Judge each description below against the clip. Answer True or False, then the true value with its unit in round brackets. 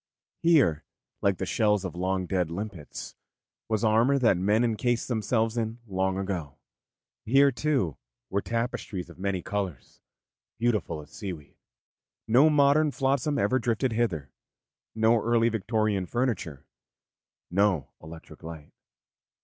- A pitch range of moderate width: True (4.6 semitones)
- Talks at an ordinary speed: False (125 wpm)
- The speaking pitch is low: True (105 Hz)